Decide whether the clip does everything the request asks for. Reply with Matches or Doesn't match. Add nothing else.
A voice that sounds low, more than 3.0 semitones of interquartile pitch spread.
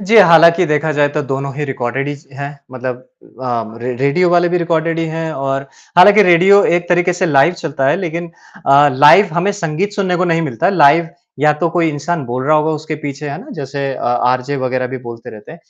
Doesn't match